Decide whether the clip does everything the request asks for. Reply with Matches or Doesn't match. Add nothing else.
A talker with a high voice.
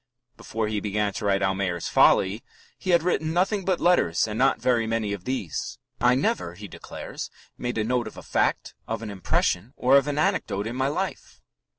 Doesn't match